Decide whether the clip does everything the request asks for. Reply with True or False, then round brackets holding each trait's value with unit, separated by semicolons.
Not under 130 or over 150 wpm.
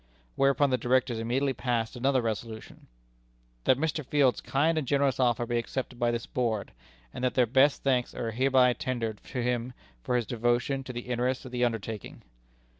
False (180 wpm)